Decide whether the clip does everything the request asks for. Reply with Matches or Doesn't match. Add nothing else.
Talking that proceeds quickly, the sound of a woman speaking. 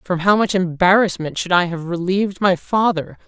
Doesn't match